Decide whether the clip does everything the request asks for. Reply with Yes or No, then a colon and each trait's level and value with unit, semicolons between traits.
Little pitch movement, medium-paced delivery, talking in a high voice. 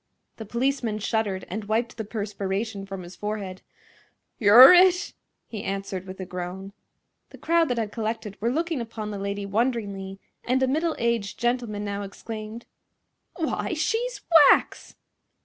No: average, 3.5 semitones; average, 150 wpm; high, 215 Hz